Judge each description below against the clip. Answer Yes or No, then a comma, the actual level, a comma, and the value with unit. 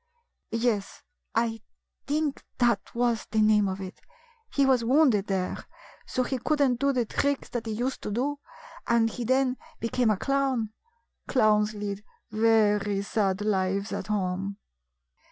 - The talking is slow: No, average, 150 wpm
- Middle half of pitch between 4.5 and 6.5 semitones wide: No, average, 3.7 semitones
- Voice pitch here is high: Yes, high, 225 Hz